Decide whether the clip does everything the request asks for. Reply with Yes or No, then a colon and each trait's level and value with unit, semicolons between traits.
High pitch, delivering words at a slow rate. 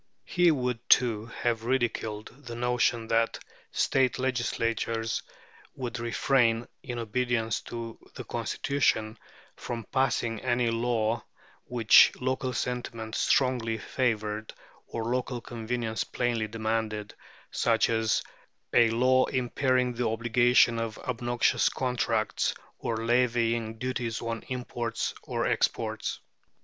No: low, 120 Hz; slow, 110 wpm